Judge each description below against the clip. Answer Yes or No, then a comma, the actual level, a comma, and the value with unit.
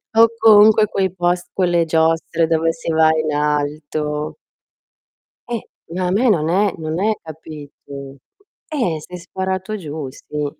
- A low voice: No, medium, 165 Hz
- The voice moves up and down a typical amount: Yes, average, 3.7 semitones